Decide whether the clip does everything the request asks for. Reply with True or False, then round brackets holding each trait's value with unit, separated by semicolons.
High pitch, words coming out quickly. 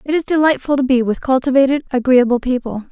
False (260 Hz; 185 wpm)